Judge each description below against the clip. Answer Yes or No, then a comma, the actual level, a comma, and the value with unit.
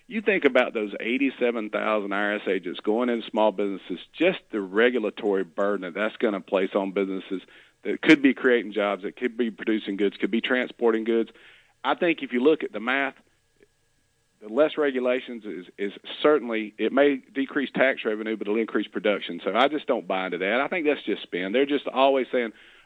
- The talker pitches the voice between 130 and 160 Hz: No, low, 115 Hz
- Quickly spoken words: No, average, 195 wpm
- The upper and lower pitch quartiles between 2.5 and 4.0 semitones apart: No, average, 4.5 semitones